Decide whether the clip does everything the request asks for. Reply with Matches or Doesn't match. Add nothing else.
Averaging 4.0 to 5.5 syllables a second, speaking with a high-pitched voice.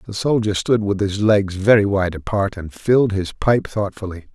Doesn't match